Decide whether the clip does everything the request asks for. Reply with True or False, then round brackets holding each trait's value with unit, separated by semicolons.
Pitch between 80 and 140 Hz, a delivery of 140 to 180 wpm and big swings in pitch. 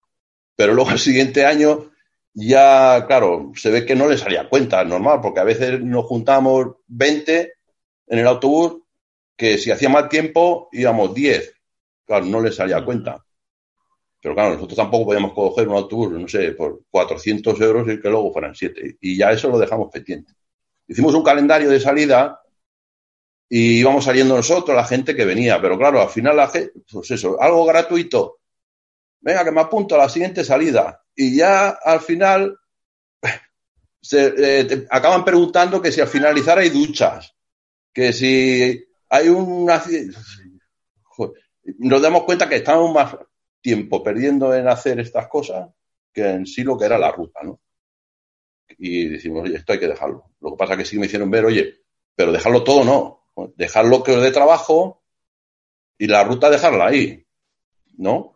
True (135 Hz; 170 wpm; 6.5 semitones)